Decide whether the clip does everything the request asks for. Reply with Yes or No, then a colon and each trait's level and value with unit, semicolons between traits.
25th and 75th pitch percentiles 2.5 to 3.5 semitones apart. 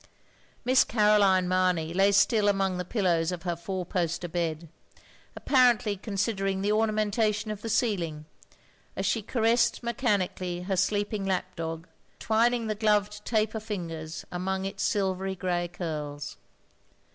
Yes: average, 3.2 semitones